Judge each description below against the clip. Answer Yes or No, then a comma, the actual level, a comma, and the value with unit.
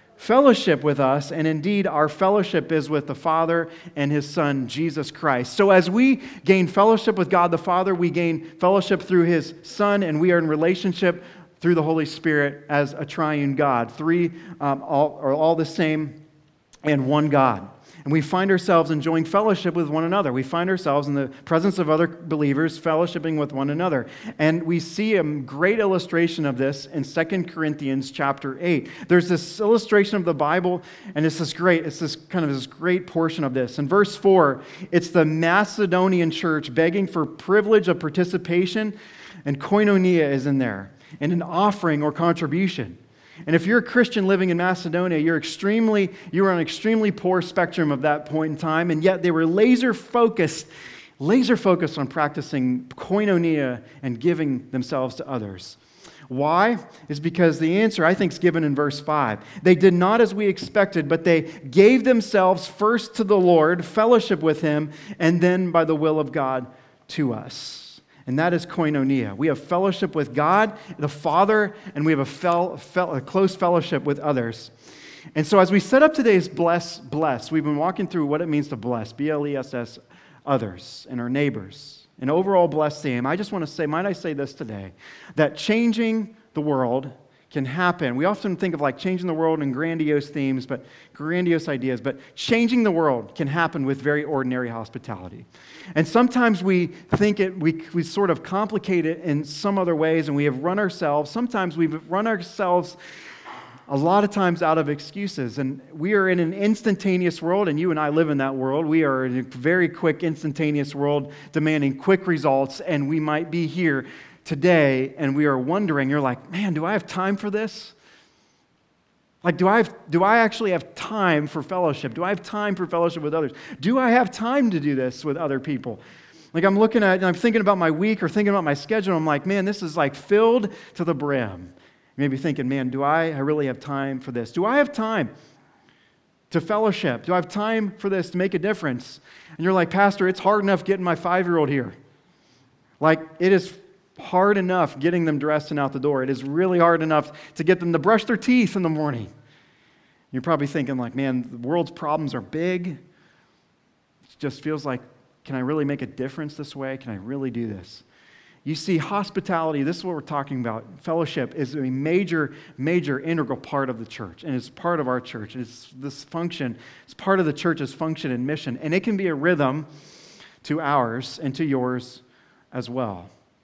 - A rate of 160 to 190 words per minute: No, average, 200 wpm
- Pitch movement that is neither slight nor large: Yes, average, 4.5 semitones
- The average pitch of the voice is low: No, medium, 160 Hz